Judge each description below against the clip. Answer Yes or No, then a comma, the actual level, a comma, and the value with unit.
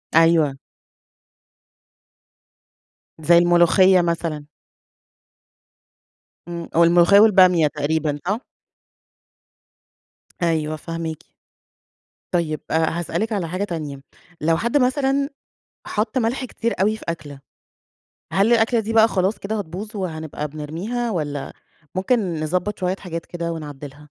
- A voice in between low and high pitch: Yes, medium, 175 Hz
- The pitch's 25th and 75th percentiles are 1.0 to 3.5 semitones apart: No, average, 4.7 semitones